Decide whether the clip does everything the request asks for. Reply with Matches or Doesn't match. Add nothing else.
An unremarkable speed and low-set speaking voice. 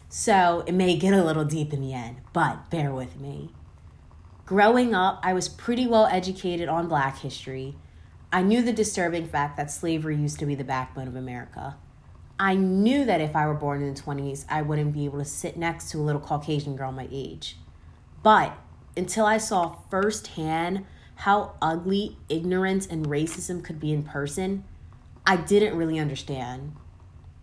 Doesn't match